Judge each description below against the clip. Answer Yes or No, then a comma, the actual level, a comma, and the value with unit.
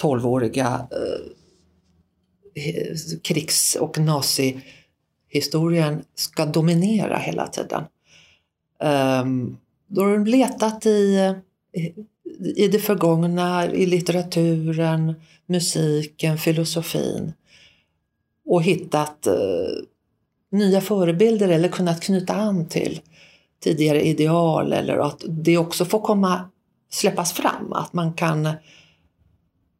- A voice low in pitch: No, medium, 165 Hz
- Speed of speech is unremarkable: No, slow, 95 wpm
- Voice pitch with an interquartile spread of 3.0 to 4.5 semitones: Yes, average, 4.0 semitones